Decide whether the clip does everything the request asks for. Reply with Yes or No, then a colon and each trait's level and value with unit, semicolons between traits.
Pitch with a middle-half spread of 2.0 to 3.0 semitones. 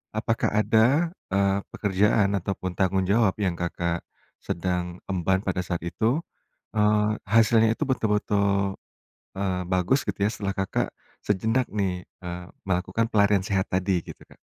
Yes: average, 2.7 semitones